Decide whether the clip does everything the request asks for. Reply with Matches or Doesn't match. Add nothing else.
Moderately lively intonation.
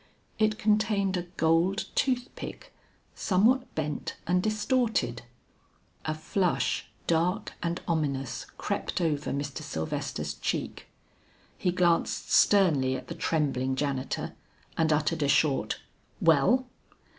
Doesn't match